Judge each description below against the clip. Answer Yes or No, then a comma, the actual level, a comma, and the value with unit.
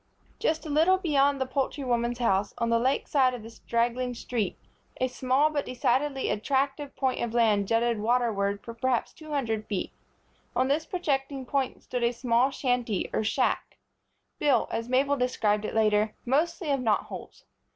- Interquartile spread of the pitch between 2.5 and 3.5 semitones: Yes, average, 3.1 semitones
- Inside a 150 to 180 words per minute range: Yes, average, 170 wpm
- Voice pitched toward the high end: Yes, very high, 250 Hz